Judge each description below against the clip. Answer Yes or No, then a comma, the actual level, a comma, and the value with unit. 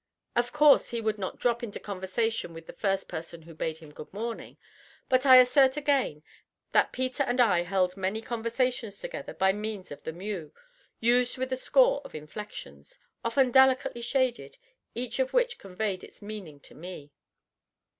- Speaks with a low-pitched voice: No, high, 220 Hz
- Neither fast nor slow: Yes, average, 175 wpm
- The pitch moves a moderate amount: No, wide, 5.7 semitones